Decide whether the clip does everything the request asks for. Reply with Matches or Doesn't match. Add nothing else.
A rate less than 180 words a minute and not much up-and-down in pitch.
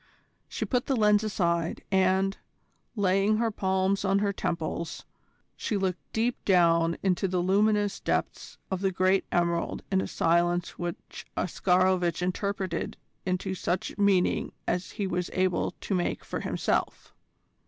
Matches